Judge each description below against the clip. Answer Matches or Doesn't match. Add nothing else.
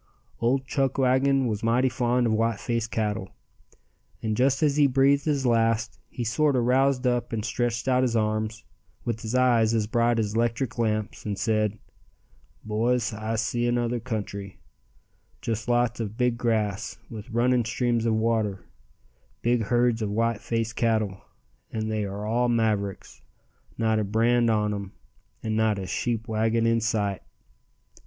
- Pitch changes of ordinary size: Doesn't match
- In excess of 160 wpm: Doesn't match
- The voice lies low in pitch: Matches